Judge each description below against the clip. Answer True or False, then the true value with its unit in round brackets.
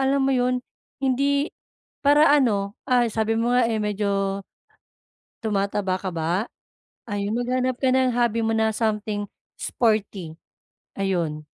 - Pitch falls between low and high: False (220 Hz)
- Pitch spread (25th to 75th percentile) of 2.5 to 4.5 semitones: True (4.0 semitones)